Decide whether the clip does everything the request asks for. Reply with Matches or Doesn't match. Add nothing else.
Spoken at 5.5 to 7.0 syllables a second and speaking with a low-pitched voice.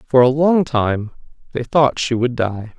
Doesn't match